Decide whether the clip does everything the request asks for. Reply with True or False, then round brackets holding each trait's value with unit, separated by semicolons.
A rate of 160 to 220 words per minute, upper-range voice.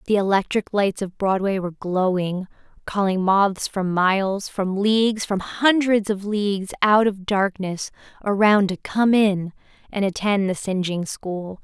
False (145 wpm; 195 Hz)